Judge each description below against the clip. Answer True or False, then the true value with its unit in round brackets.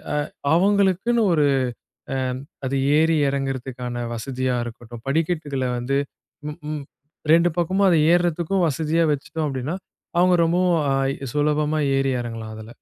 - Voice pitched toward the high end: False (150 Hz)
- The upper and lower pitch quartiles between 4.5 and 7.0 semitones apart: True (4.9 semitones)